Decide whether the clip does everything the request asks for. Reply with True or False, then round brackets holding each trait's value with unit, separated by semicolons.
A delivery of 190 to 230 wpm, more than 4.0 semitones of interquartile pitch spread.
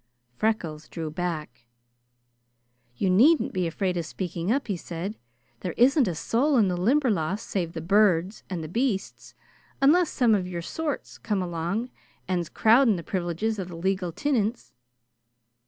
False (155 wpm; 5.0 semitones)